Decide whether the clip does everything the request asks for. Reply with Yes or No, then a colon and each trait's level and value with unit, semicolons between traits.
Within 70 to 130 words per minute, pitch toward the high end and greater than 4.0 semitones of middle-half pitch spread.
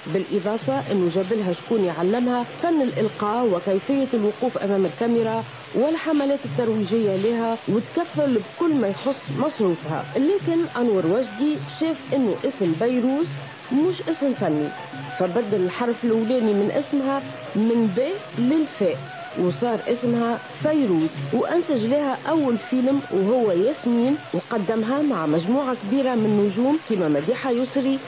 Yes: average, 120 wpm; high, 235 Hz; average, 5.2 semitones